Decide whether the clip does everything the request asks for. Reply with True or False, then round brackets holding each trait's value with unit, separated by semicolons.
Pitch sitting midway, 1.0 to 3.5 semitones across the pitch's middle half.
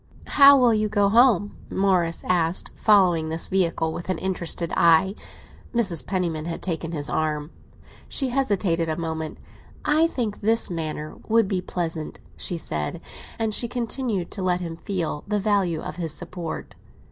False (180 Hz; 4.4 semitones)